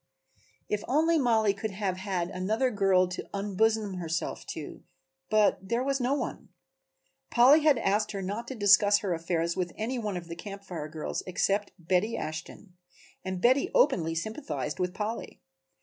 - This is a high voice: Yes, high, 200 Hz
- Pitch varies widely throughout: No, average, 3.8 semitones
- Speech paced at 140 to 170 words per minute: Yes, average, 165 wpm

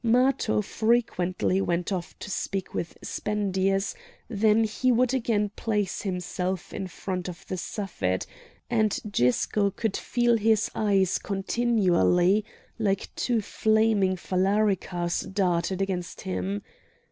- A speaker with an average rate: No, slow, 115 wpm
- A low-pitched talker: No, high, 195 Hz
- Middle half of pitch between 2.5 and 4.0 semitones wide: Yes, average, 3.1 semitones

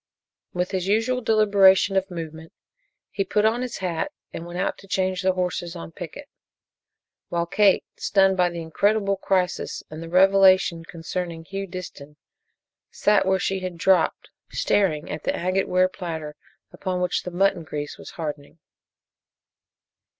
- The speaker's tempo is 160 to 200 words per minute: No, average, 150 wpm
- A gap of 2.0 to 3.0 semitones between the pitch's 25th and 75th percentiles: Yes, average, 2.7 semitones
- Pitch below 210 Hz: Yes, medium, 185 Hz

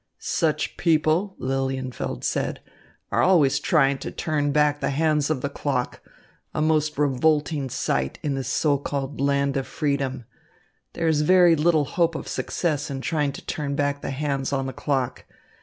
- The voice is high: No, medium, 145 Hz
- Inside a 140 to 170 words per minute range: Yes, average, 165 wpm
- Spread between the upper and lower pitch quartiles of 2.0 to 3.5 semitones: Yes, narrow, 2.4 semitones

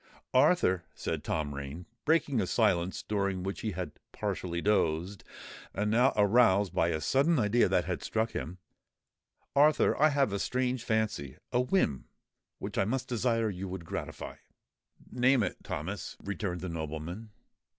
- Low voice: Yes, low, 100 Hz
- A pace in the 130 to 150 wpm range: Yes, average, 145 wpm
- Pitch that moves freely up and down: Yes, wide, 5.7 semitones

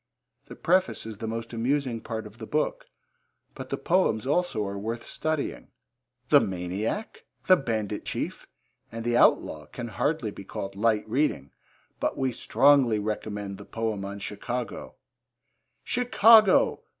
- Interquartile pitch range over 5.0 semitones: Yes, wide, 5.4 semitones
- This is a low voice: Yes, low, 115 Hz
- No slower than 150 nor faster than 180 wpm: No, average, 140 wpm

